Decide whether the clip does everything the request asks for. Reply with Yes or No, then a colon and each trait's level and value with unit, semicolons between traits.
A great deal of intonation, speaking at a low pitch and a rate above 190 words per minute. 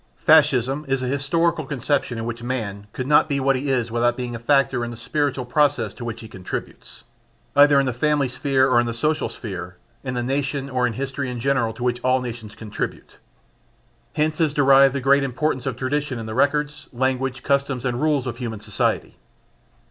No: average, 2.8 semitones; low, 130 Hz; average, 200 wpm